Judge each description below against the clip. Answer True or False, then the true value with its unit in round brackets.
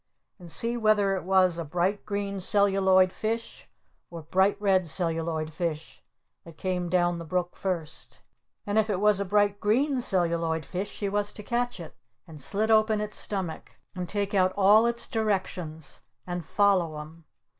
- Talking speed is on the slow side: False (170 wpm)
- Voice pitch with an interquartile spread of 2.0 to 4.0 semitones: True (3.4 semitones)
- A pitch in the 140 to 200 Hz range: True (190 Hz)